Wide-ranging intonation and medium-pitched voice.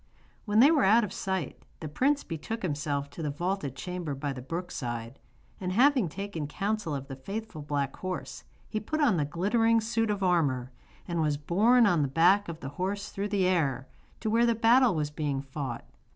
Yes: wide, 6.7 semitones; medium, 180 Hz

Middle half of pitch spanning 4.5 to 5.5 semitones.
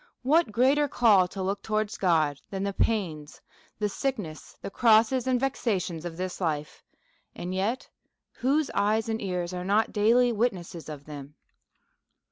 Yes: average, 5.1 semitones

